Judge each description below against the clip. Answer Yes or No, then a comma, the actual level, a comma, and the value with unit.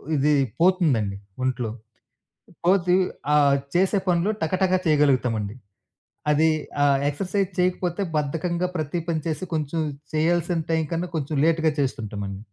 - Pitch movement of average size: Yes, average, 4.0 semitones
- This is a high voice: No, medium, 160 Hz